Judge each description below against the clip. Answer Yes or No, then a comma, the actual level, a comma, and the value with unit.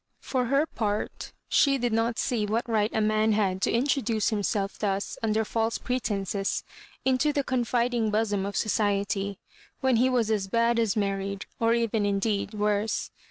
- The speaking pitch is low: No, high, 220 Hz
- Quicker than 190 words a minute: No, average, 170 wpm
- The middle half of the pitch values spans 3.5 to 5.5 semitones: No, narrow, 2.6 semitones